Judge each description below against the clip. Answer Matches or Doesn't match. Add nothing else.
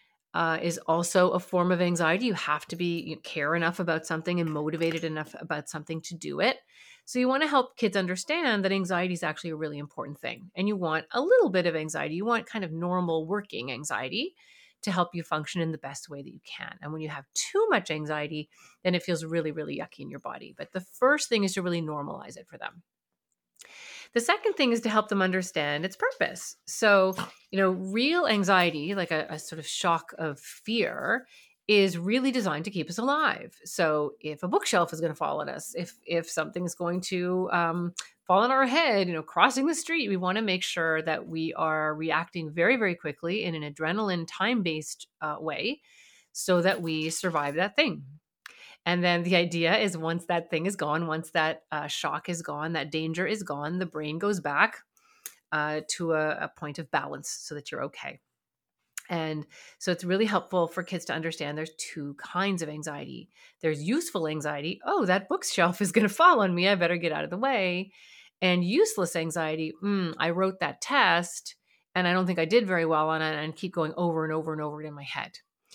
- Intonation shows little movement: Doesn't match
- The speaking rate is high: Matches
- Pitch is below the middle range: Doesn't match